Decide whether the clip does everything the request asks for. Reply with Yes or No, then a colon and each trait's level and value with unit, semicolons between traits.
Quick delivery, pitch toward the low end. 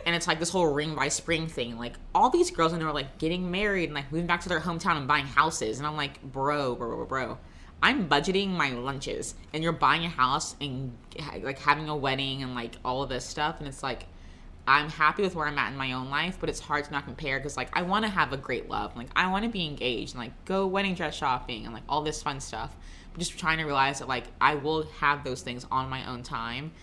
No: fast, 255 wpm; medium, 145 Hz